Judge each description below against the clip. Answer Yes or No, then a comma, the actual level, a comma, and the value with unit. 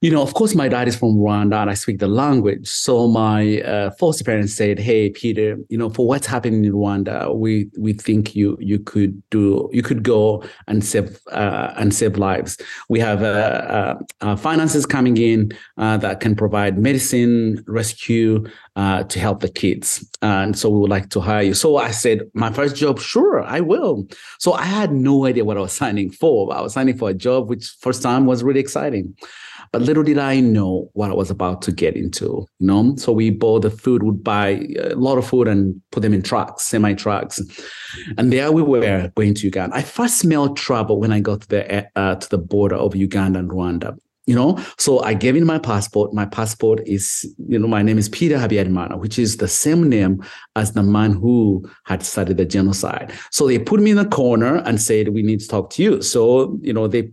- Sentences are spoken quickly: Yes, fast, 220 wpm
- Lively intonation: No, average, 3.4 semitones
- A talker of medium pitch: No, low, 110 Hz